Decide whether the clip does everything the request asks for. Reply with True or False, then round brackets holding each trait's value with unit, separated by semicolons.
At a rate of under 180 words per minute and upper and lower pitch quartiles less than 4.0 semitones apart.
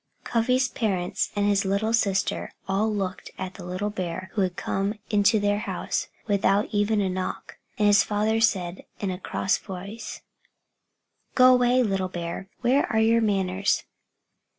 True (155 wpm; 2.6 semitones)